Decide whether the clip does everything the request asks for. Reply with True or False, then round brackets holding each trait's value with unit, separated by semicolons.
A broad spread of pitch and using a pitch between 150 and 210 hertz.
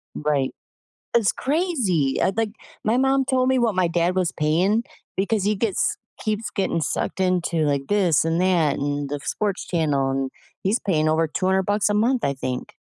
True (5.7 semitones; 185 Hz)